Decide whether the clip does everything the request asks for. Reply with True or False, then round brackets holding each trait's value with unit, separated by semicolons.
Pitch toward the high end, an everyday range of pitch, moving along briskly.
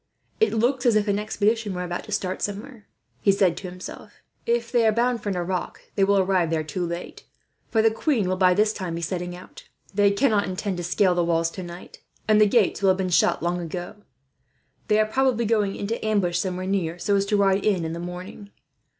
True (195 Hz; 3.3 semitones; 215 wpm)